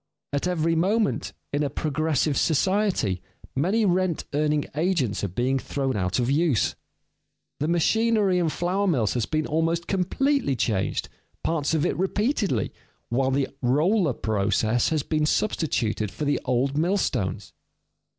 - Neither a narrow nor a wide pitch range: No, wide, 5.9 semitones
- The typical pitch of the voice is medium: Yes, medium, 155 Hz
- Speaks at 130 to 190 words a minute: Yes, average, 140 wpm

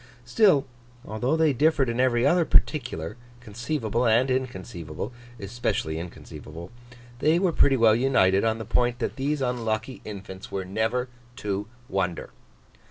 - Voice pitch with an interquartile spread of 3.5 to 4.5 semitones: No, average, 4.9 semitones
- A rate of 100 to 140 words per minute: Yes, slow, 135 wpm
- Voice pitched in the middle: No, low, 120 Hz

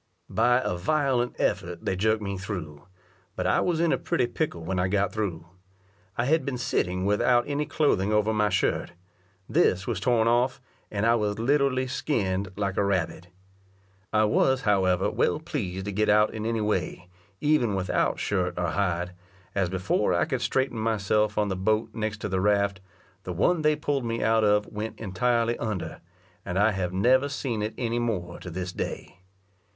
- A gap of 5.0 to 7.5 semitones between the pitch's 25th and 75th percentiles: No, average, 4.3 semitones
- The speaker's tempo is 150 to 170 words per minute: No, average, 185 wpm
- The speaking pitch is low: Yes, low, 105 Hz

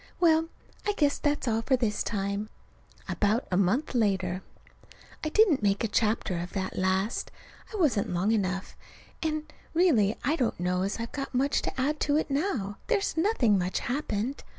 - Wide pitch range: Yes, wide, 7.2 semitones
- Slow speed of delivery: No, average, 175 wpm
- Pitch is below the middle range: No, high, 230 Hz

